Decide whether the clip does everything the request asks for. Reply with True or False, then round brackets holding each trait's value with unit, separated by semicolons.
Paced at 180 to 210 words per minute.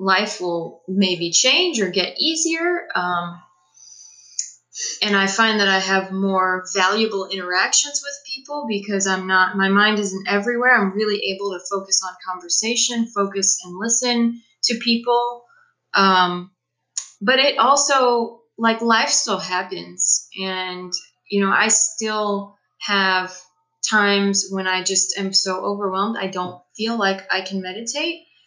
False (140 wpm)